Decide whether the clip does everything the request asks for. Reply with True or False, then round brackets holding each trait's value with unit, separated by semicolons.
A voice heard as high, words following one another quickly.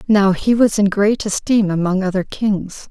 False (200 Hz; 185 wpm)